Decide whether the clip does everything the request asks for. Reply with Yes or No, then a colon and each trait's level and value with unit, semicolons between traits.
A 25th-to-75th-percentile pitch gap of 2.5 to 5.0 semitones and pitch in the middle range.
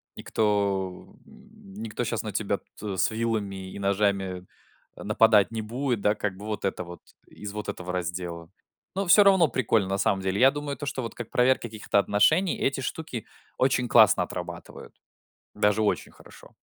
No: average, 3.8 semitones; low, 105 Hz